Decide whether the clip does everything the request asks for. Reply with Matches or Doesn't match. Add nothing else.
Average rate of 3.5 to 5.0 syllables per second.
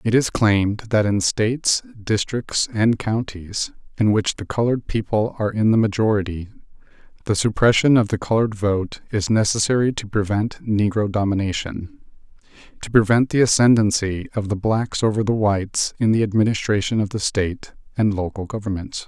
Doesn't match